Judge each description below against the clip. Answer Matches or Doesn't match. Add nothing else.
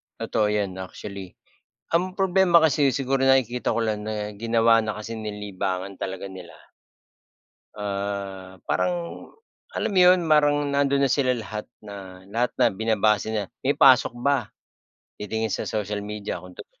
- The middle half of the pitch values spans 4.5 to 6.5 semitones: Matches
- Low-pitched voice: Matches